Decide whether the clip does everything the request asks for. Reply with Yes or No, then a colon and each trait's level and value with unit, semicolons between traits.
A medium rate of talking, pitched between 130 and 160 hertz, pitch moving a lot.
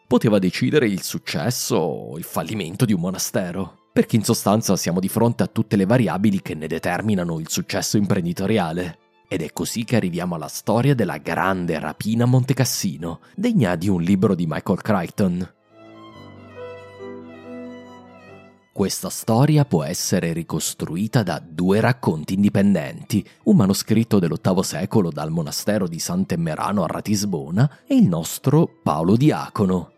No: average, 135 wpm; low, 100 Hz; wide, 5.7 semitones